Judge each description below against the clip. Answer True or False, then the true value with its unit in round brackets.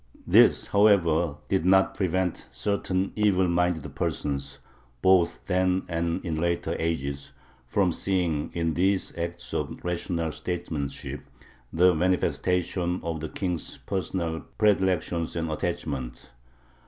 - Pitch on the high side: False (85 Hz)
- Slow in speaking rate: True (115 wpm)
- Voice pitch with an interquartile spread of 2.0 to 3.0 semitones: True (2.4 semitones)